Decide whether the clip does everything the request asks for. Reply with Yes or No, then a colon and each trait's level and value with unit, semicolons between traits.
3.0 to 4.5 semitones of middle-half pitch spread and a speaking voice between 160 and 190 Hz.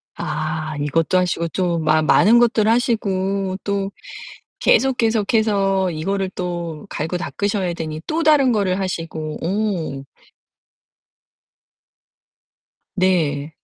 Yes: average, 4.1 semitones; medium, 185 Hz